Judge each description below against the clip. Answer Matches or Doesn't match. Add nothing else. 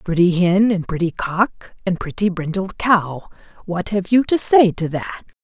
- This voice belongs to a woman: Matches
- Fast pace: Doesn't match